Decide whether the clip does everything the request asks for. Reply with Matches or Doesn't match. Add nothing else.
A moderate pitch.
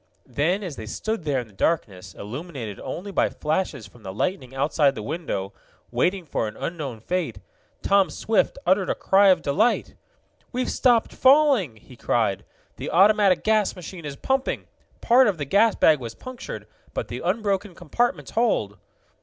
Matches